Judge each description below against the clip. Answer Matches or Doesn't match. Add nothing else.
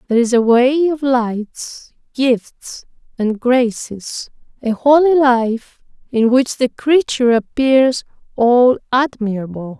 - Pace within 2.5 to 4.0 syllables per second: Matches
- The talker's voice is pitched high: Matches